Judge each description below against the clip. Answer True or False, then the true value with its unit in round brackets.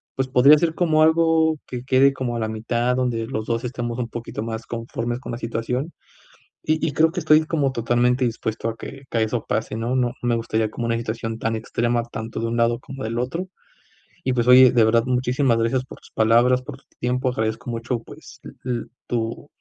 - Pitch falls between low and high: False (120 Hz)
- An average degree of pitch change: False (2.2 semitones)